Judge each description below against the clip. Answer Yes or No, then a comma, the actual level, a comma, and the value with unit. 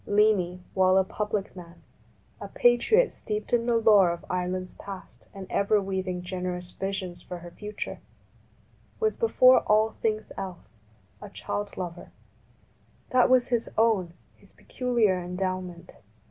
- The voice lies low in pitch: No, high, 195 Hz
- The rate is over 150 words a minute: No, slow, 135 wpm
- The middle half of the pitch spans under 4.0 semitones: Yes, average, 3.3 semitones